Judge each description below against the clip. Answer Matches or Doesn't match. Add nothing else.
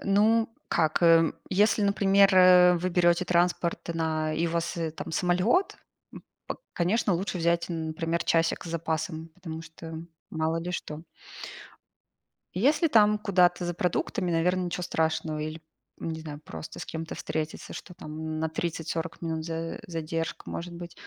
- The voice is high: Doesn't match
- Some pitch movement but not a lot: Doesn't match